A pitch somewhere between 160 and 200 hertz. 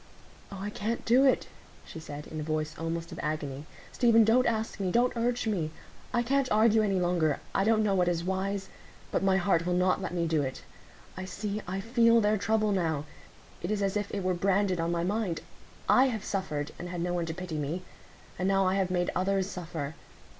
Yes: high, 190 Hz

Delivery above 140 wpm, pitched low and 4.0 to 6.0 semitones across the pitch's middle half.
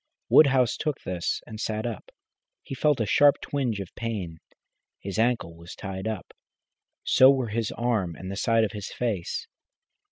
Yes: average, 165 wpm; low, 110 Hz; average, 4.3 semitones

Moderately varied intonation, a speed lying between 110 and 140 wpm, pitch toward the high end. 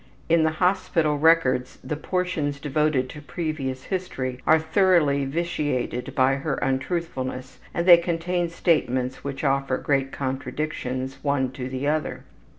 No: average, 3.9 semitones; slow, 135 wpm; medium, 145 Hz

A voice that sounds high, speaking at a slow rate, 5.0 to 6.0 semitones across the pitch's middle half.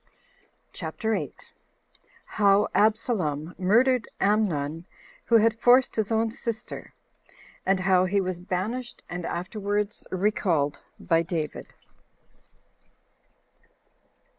No: high, 200 Hz; slow, 90 wpm; average, 3.8 semitones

